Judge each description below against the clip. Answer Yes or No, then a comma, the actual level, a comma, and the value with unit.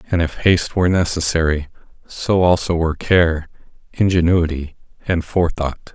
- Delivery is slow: Yes, slow, 120 wpm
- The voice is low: Yes, very low, 85 Hz